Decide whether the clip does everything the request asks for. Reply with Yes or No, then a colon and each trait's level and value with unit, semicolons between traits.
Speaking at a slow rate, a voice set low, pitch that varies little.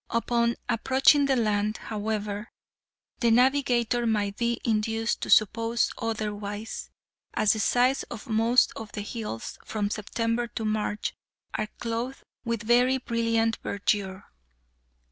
No: slow, 125 wpm; high, 225 Hz; narrow, 1.9 semitones